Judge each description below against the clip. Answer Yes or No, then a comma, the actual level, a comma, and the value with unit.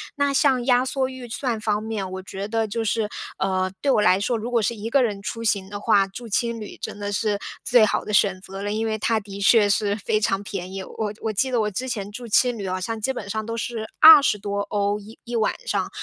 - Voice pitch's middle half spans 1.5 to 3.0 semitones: Yes, average, 2.7 semitones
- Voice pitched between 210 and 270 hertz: Yes, high, 215 Hz